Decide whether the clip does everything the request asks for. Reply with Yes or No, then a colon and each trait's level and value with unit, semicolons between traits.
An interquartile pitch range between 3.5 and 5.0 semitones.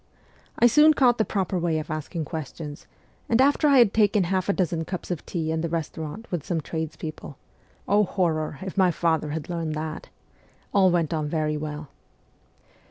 Yes: average, 3.9 semitones